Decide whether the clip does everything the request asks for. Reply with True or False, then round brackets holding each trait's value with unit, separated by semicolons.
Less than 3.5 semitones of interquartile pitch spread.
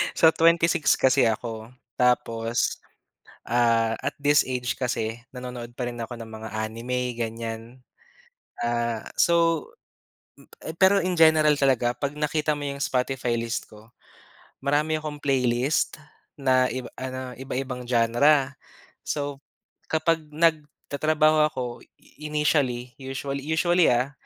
False (4.1 semitones)